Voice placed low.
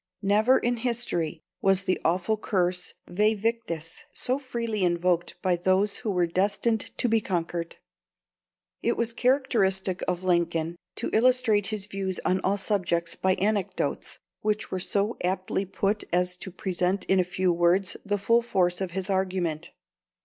No: high, 190 Hz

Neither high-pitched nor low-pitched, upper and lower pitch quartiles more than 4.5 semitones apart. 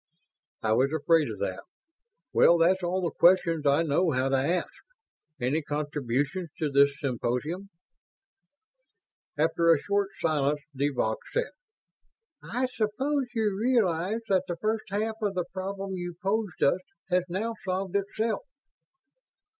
Yes: medium, 175 Hz; wide, 5.4 semitones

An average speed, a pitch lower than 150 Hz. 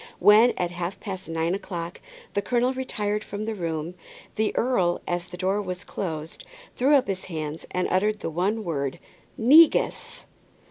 No: average, 160 wpm; high, 190 Hz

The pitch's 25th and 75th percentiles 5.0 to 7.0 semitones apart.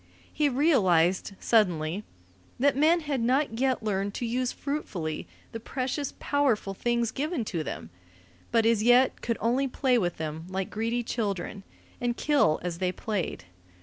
Yes: wide, 5.6 semitones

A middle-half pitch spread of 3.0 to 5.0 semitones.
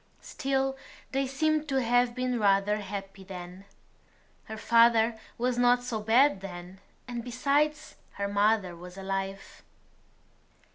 Yes: average, 4.5 semitones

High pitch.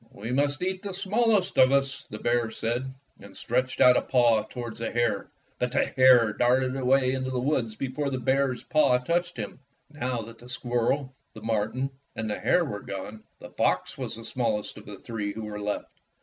No: low, 125 Hz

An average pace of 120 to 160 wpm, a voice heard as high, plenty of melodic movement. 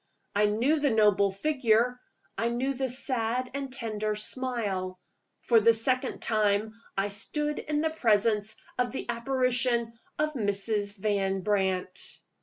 No: slow, 135 wpm; high, 230 Hz; average, 3.8 semitones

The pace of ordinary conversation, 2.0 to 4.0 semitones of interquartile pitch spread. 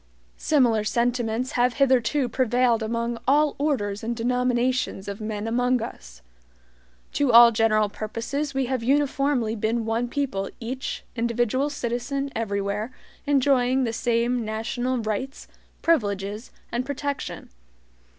No: slow, 120 wpm; average, 2.7 semitones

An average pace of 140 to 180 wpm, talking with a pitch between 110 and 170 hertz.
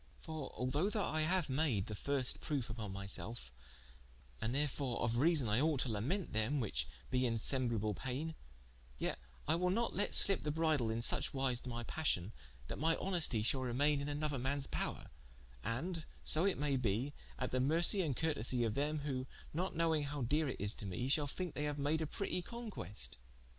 No: average, 200 wpm; medium, 140 Hz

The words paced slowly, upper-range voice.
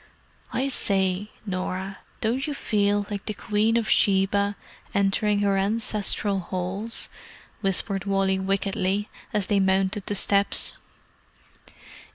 Yes: slow, 115 wpm; high, 200 Hz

